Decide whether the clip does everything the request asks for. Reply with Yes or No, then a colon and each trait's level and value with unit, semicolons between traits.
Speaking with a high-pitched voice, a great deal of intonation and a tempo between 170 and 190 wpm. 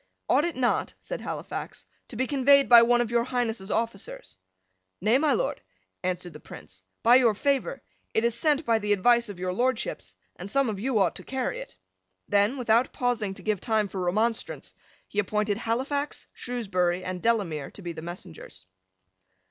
No: high, 225 Hz; average, 4.6 semitones; average, 180 wpm